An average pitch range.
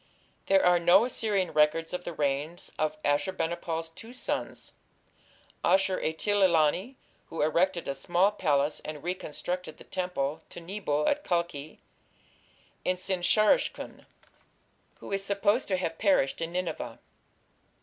Yes: average, 3.7 semitones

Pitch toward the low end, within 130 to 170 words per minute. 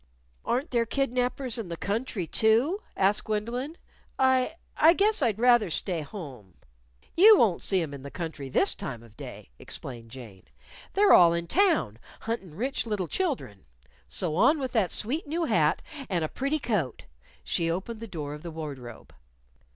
No: high, 210 Hz; average, 165 wpm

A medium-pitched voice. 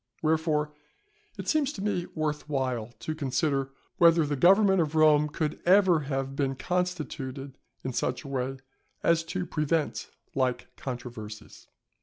Yes: medium, 150 Hz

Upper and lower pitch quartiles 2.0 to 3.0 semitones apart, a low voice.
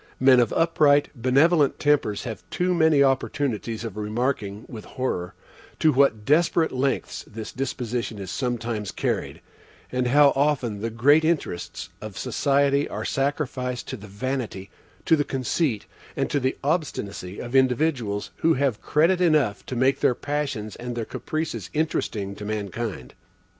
No: average, 5.0 semitones; low, 130 Hz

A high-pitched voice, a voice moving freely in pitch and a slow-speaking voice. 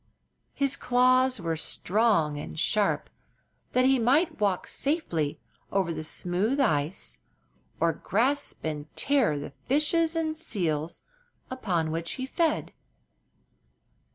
Yes: high, 210 Hz; wide, 8.7 semitones; slow, 115 wpm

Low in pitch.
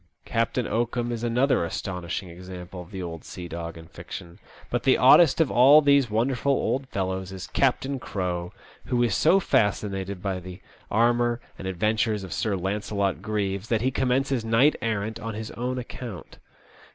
Yes: low, 110 Hz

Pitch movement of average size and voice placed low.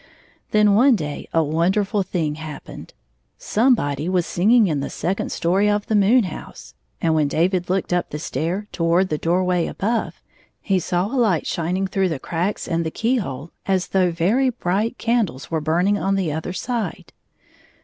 No: average, 4.0 semitones; medium, 185 Hz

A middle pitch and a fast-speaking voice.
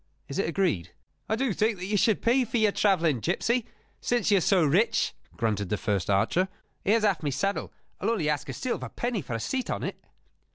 No: high, 195 Hz; fast, 215 wpm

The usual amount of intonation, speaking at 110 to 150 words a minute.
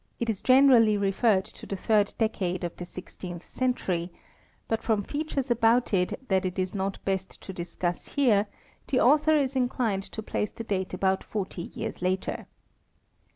No: average, 4.6 semitones; average, 160 wpm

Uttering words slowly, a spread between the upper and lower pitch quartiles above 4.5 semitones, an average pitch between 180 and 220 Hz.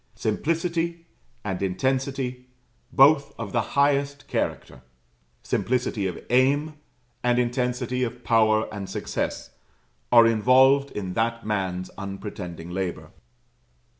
No: slow, 105 wpm; average, 4.9 semitones; low, 120 Hz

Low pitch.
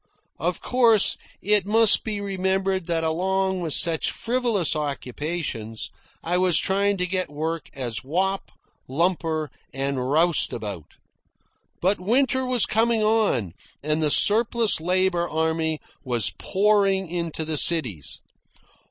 No: medium, 175 Hz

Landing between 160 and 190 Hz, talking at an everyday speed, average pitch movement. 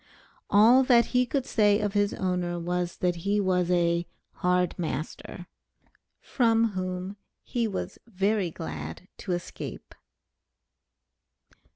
No: medium, 185 Hz; slow, 115 wpm; average, 3.2 semitones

